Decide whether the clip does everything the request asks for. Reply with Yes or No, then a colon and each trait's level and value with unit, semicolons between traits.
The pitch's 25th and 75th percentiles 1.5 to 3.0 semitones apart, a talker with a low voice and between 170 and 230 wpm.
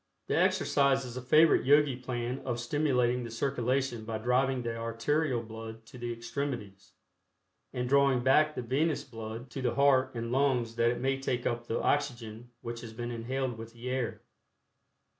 Yes: narrow, 2.5 semitones; low, 125 Hz; average, 175 wpm